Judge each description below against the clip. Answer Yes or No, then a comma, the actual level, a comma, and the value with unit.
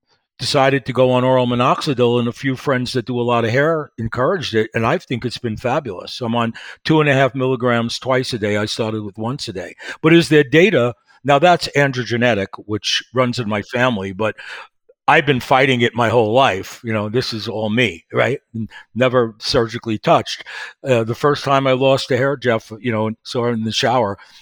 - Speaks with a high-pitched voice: No, low, 125 Hz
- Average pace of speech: No, fast, 210 wpm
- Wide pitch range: No, average, 2.9 semitones